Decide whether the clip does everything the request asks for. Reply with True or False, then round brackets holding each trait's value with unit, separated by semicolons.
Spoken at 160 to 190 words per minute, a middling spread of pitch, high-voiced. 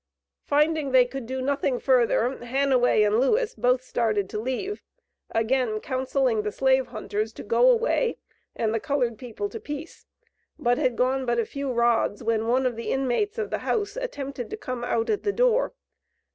True (180 wpm; 3.7 semitones; 255 Hz)